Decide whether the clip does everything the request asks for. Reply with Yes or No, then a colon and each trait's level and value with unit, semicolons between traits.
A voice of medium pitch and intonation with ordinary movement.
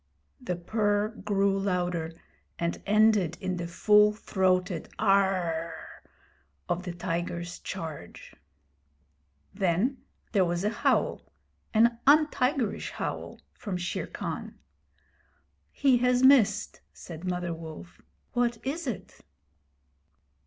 No: high, 195 Hz; average, 4.1 semitones